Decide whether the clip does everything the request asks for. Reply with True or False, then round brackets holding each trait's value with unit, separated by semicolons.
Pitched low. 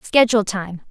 False (210 Hz)